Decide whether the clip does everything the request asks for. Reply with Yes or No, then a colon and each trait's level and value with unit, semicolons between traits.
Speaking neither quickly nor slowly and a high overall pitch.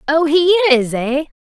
Yes: average, 170 wpm; very high, 300 Hz